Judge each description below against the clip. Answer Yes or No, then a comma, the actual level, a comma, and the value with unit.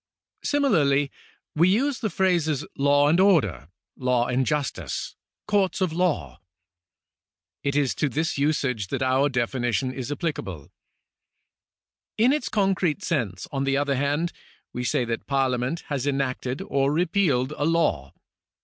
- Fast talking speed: No, average, 140 wpm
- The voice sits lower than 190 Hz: Yes, medium, 140 Hz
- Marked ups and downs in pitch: No, average, 4.9 semitones